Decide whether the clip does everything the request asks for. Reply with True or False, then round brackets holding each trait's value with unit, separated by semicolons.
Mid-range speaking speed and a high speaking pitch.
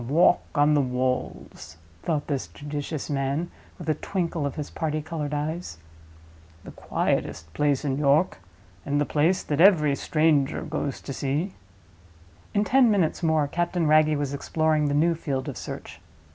False (160 wpm; 150 Hz)